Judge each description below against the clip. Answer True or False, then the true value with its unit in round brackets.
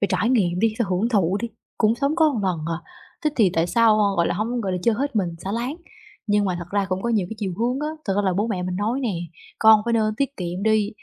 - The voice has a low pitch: False (215 Hz)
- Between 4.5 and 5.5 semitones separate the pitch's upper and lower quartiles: False (3.9 semitones)